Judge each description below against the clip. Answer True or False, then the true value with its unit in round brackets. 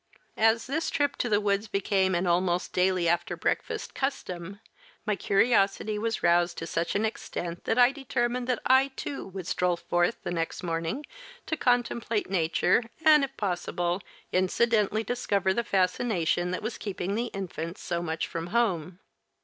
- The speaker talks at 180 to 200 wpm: False (160 wpm)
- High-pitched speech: True (195 Hz)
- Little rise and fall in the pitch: False (5.1 semitones)